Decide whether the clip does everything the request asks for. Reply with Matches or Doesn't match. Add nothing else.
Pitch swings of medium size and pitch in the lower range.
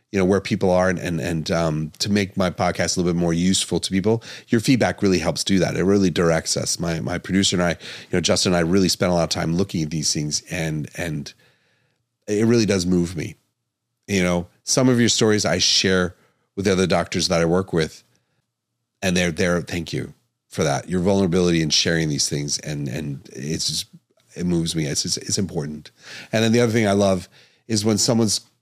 Matches